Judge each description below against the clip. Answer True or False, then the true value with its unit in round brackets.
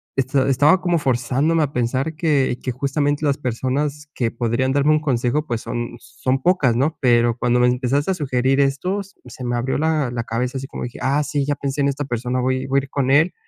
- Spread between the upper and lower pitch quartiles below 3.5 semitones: True (2.9 semitones)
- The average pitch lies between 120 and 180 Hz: True (135 Hz)